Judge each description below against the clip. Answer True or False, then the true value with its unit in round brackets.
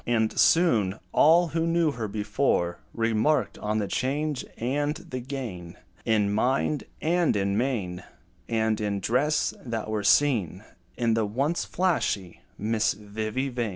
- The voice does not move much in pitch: False (5.3 semitones)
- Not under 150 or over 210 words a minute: False (140 wpm)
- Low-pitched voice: True (115 Hz)